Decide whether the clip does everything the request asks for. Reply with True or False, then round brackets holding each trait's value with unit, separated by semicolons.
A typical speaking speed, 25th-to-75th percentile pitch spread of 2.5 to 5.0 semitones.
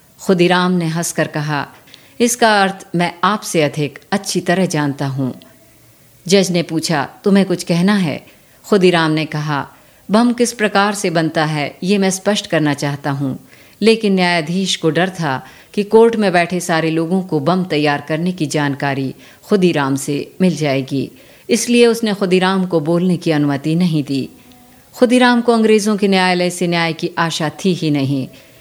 True (160 wpm; 4.4 semitones)